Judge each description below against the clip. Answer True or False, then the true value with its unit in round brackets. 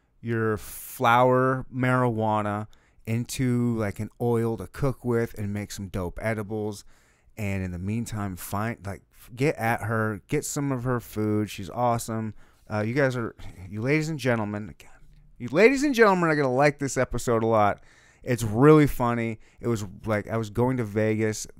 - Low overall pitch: True (115 Hz)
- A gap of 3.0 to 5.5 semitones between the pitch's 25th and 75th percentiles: True (3.3 semitones)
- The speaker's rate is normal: True (170 wpm)